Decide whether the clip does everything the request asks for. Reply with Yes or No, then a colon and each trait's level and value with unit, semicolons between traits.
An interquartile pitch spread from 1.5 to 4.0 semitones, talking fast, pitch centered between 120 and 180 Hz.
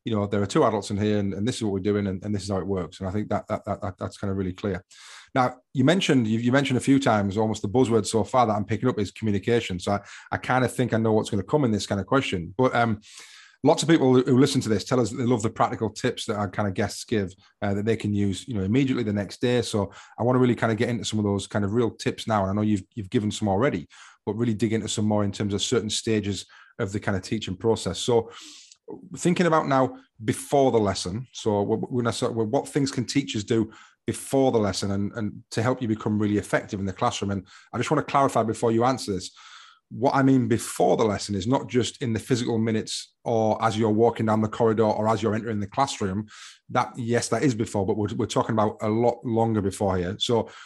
No: average, 3.1 semitones; fast, 270 wpm; low, 110 Hz